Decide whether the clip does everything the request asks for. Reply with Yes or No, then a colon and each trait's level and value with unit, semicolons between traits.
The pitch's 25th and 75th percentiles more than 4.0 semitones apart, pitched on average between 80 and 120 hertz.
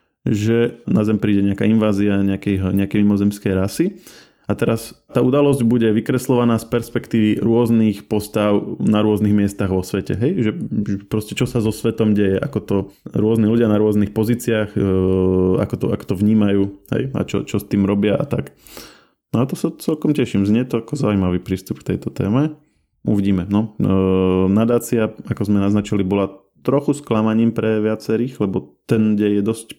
No: narrow, 2.4 semitones; low, 105 Hz